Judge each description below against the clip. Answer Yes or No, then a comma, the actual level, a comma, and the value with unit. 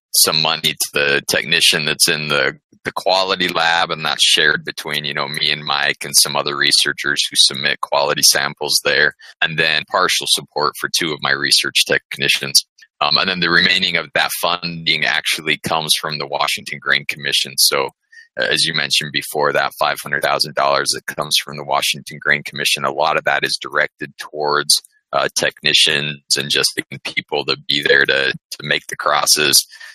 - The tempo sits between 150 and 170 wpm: No, average, 185 wpm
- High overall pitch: No, very low, 85 Hz